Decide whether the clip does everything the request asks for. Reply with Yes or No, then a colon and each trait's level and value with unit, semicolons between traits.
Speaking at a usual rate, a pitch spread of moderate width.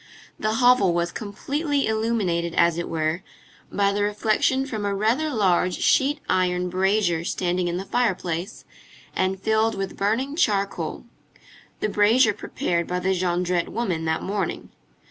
Yes: average, 145 wpm; average, 3.8 semitones